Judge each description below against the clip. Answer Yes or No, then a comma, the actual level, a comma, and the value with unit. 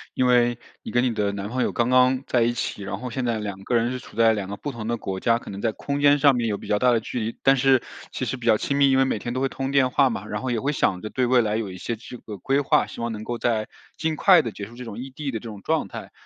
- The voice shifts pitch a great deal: No, average, 3.2 semitones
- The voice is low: Yes, low, 120 Hz